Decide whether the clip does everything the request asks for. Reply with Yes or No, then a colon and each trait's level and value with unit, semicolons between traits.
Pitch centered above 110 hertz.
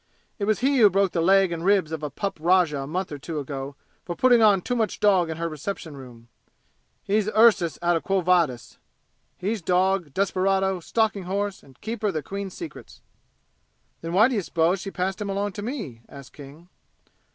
Yes: medium, 185 Hz